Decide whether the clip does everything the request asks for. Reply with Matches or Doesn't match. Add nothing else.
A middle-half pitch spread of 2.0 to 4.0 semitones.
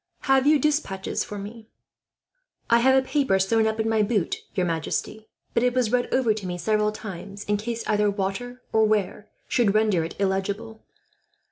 Matches